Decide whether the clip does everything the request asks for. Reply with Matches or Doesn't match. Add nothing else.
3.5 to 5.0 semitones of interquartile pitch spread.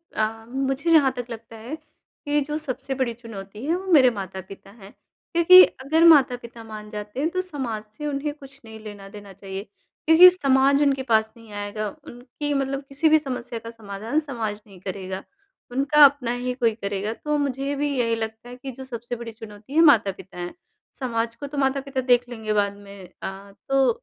Matches